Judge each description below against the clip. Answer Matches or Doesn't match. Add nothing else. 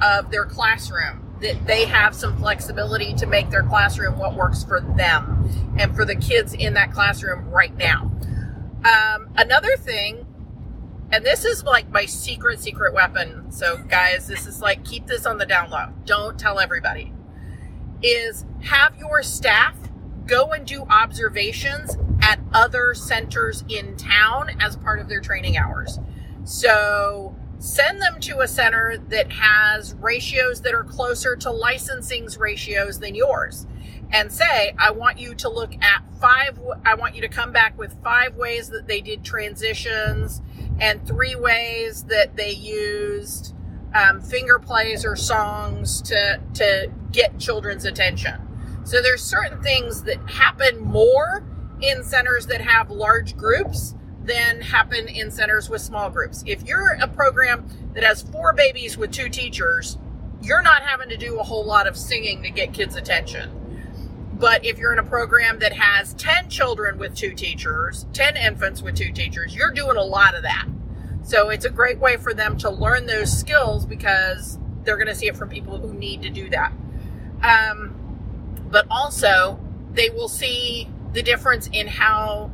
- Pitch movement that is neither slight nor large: Doesn't match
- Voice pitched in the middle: Doesn't match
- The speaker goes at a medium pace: Matches